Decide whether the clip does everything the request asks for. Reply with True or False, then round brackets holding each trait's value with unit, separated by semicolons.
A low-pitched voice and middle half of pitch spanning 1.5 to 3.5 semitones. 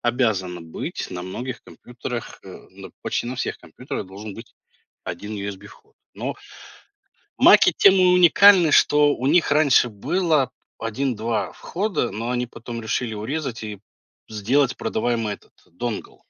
False (120 Hz; 5.0 semitones)